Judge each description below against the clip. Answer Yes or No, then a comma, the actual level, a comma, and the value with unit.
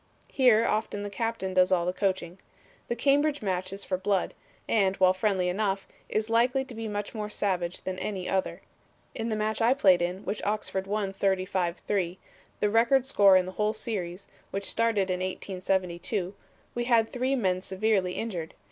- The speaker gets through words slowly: No, average, 180 wpm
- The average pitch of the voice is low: No, high, 200 Hz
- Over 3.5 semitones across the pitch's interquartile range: No, average, 3.2 semitones